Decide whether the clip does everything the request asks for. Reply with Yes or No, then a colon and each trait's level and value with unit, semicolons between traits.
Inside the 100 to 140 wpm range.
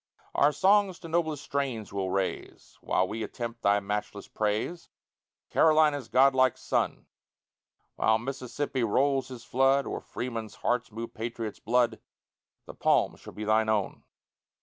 Yes: slow, 135 wpm